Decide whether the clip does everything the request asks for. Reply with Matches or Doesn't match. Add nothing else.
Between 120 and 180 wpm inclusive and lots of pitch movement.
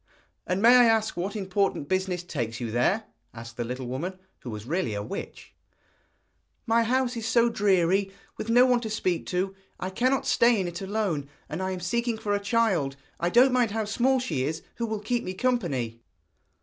Doesn't match